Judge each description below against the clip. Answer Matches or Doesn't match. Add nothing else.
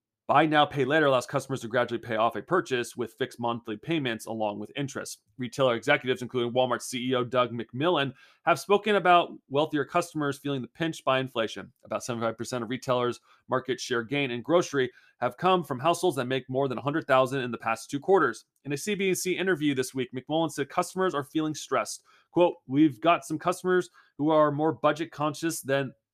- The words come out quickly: Doesn't match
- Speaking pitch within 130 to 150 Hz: Matches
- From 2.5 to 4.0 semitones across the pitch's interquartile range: Doesn't match